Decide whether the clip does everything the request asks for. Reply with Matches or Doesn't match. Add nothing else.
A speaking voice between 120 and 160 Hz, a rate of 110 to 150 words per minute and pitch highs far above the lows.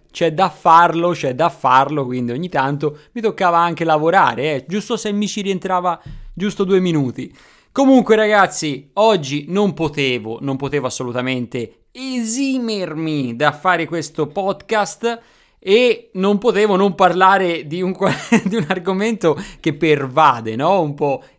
Doesn't match